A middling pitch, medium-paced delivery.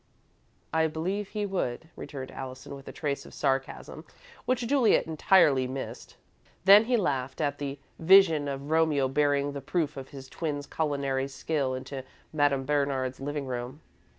Yes: medium, 145 Hz; average, 150 wpm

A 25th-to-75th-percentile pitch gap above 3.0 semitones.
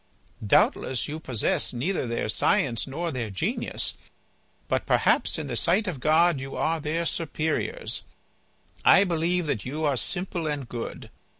Yes: average, 4.9 semitones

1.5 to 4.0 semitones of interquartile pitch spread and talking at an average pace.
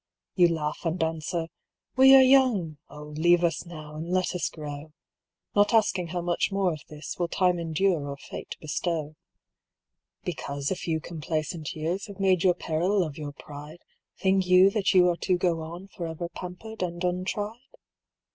Yes: average, 3.0 semitones; average, 170 wpm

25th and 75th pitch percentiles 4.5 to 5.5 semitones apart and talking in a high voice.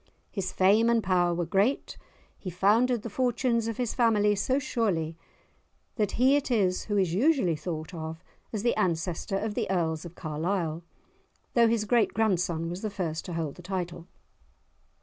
Yes: average, 4.9 semitones; high, 195 Hz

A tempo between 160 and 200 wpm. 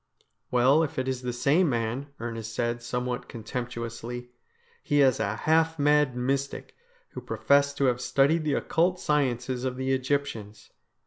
Yes: average, 170 wpm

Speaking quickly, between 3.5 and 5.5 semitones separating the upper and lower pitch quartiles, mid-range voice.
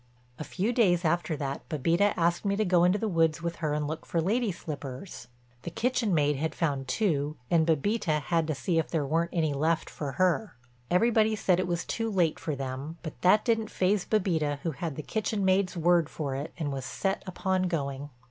Yes: fast, 210 wpm; average, 4.0 semitones; medium, 170 Hz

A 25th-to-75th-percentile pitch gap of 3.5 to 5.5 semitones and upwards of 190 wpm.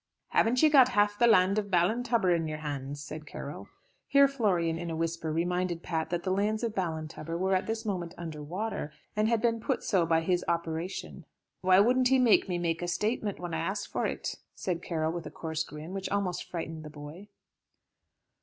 Yes: average, 4.3 semitones; average, 200 wpm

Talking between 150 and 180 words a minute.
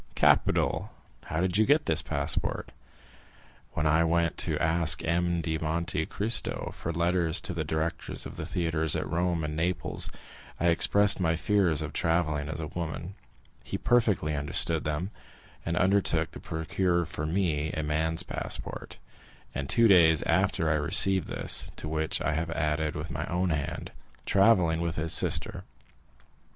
Yes: average, 160 wpm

